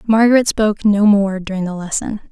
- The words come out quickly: No, average, 180 wpm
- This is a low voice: No, high, 205 Hz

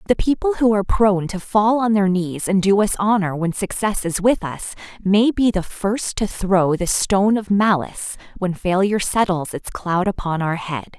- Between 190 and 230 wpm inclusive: Yes, average, 200 wpm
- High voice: Yes, high, 195 Hz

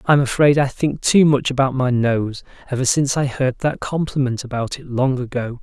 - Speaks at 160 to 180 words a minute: No, fast, 205 wpm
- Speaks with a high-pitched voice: No, low, 130 Hz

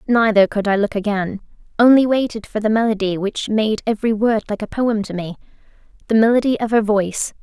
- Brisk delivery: No, average, 195 wpm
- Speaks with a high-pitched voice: Yes, high, 215 Hz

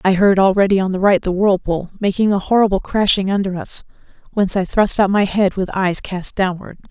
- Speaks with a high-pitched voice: Yes, high, 195 Hz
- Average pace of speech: No, fast, 210 wpm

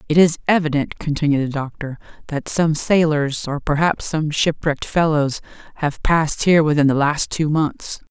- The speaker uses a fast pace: No, average, 165 wpm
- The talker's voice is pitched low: No, medium, 150 Hz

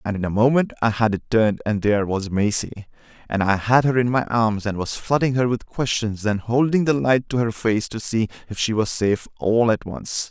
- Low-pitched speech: Yes, low, 115 Hz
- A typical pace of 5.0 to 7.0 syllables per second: Yes, 5.3 syllables/s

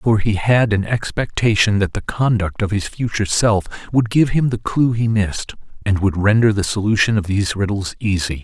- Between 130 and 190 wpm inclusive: No, average, 200 wpm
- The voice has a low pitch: Yes, low, 105 Hz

